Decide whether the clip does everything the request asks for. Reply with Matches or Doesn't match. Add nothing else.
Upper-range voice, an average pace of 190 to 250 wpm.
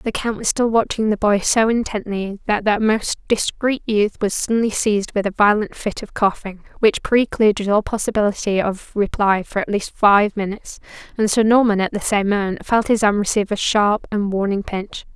Matches